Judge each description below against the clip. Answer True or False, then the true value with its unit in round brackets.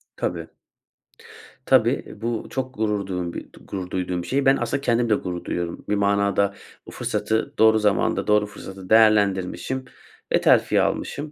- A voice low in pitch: True (105 Hz)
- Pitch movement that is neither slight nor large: True (3.3 semitones)